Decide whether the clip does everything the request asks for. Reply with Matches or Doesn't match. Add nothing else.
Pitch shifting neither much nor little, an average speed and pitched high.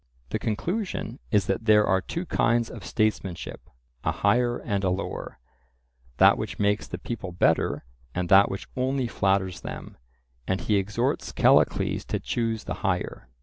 Doesn't match